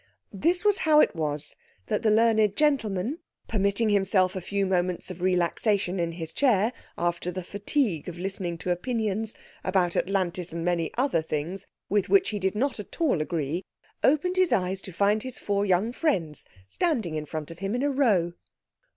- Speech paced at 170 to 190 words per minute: Yes, average, 180 wpm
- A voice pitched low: No, high, 195 Hz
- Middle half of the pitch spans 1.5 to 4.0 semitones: No, average, 4.6 semitones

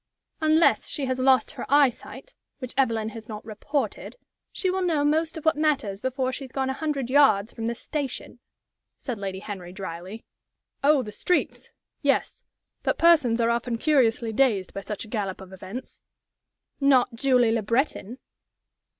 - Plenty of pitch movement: No, average, 4.8 semitones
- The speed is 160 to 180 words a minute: Yes, average, 165 wpm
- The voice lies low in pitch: No, very high, 250 Hz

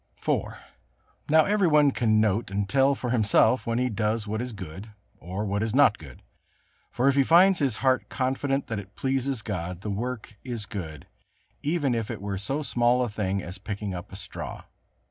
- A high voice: No, low, 115 Hz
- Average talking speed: Yes, average, 195 wpm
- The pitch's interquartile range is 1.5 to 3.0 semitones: No, average, 4.8 semitones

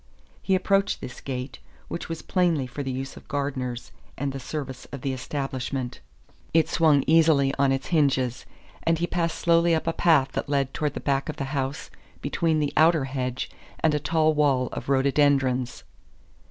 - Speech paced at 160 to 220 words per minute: Yes, average, 180 wpm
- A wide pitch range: No, average, 3.1 semitones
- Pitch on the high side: No, medium, 140 Hz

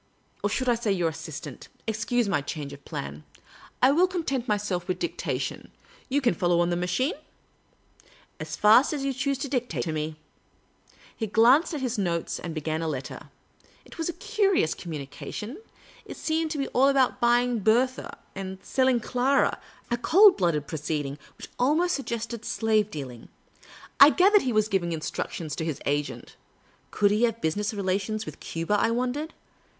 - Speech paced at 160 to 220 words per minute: Yes, average, 180 wpm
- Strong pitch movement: Yes, wide, 7.6 semitones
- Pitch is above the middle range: Yes, high, 220 Hz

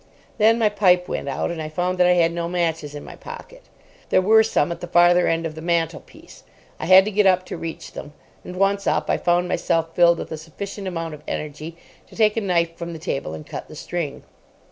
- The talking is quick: Yes, fast, 235 wpm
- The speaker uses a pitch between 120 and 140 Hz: No, medium, 175 Hz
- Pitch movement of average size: No, narrow, 2.3 semitones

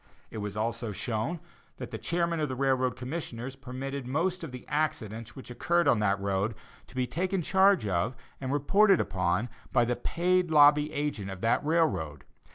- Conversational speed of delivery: Yes, average, 175 wpm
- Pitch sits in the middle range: No, low, 130 Hz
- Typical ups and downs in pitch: No, wide, 6.4 semitones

